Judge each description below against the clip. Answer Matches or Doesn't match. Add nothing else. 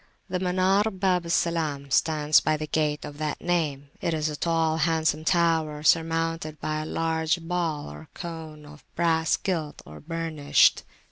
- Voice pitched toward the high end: Doesn't match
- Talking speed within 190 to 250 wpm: Doesn't match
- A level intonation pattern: Matches